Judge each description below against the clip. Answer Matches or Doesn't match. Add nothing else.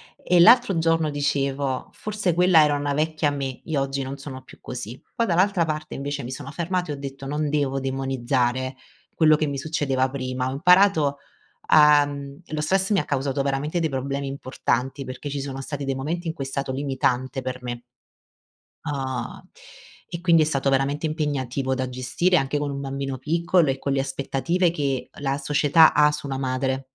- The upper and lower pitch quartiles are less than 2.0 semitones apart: Doesn't match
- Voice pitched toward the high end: Doesn't match